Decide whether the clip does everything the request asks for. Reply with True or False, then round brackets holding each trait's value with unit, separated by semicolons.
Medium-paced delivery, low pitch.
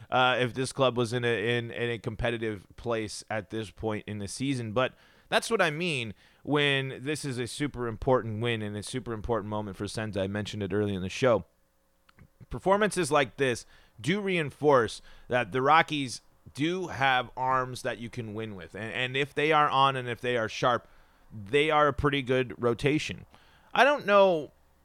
True (195 wpm; 125 Hz)